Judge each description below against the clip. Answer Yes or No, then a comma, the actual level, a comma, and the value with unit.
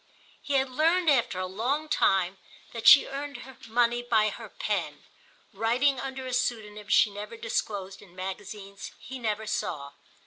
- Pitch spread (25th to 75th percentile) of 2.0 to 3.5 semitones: No, average, 4.5 semitones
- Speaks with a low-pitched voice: No, high, 225 Hz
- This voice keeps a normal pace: Yes, average, 150 wpm